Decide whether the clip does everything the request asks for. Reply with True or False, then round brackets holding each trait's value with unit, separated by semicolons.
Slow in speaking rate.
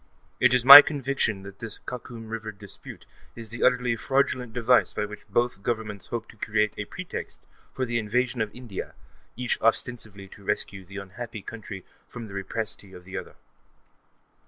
False (170 wpm)